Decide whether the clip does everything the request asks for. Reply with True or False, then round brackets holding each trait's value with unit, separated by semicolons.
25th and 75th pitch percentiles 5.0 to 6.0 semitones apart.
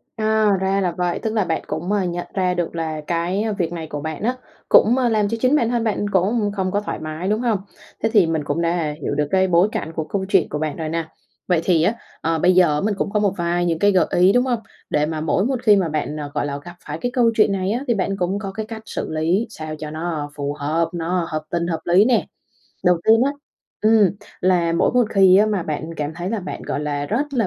False (4.6 semitones)